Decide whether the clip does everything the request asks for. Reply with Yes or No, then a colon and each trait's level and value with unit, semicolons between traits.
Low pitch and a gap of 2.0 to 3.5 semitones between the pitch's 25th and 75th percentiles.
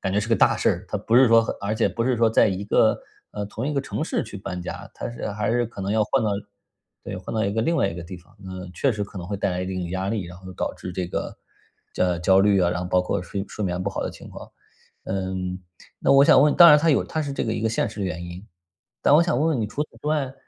No: low, 105 Hz; average, 4.5 semitones